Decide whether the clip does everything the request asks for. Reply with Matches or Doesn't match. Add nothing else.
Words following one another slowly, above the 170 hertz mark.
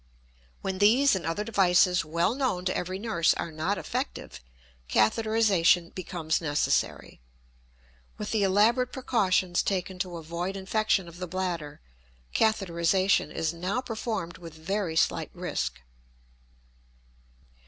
Matches